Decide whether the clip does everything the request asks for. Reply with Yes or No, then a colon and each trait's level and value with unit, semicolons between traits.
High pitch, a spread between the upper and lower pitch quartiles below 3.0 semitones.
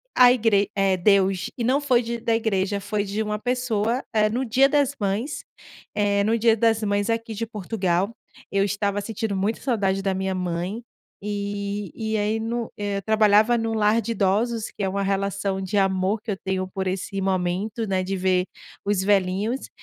Yes: high, 205 Hz; narrow, 2.6 semitones